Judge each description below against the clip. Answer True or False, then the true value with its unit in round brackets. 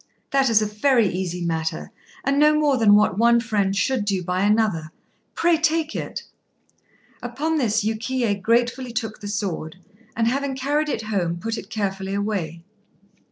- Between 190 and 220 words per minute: False (160 wpm)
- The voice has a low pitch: False (220 Hz)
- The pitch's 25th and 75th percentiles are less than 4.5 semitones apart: False (5.0 semitones)